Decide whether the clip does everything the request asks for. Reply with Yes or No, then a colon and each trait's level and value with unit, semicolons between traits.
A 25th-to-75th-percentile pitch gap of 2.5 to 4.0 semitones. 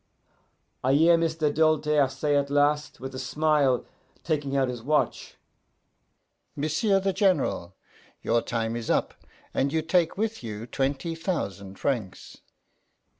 Yes: average, 3.7 semitones